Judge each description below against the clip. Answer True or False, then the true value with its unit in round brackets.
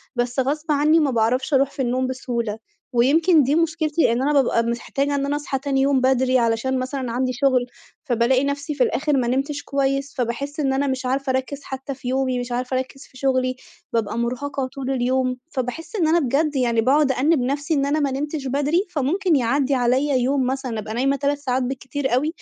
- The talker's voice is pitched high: True (265 Hz)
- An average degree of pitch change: False (2.1 semitones)